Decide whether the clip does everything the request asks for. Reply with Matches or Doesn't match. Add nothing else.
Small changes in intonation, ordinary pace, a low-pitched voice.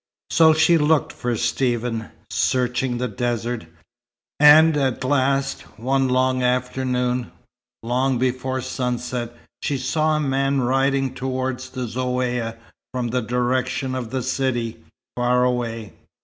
Doesn't match